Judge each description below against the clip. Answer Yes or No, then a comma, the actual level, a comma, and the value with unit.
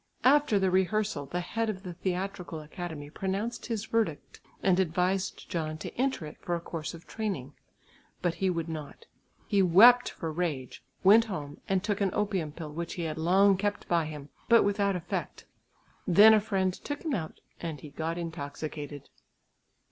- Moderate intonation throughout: Yes, average, 4.2 semitones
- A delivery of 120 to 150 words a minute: No, average, 175 wpm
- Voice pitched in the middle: Yes, medium, 180 Hz